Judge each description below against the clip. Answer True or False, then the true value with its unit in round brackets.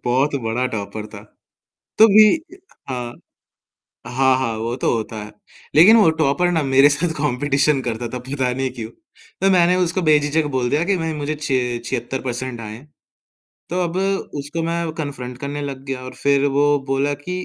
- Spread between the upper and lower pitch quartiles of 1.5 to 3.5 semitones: False (4.3 semitones)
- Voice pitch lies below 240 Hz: True (140 Hz)